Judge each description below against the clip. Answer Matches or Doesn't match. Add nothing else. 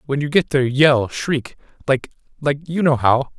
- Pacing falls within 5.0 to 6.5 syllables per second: Matches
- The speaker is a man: Matches